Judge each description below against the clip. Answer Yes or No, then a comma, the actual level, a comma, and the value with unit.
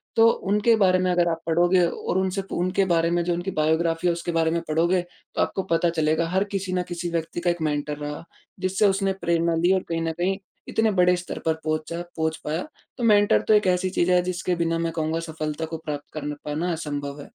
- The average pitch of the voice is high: No, medium, 170 Hz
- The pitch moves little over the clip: Yes, narrow, 2.3 semitones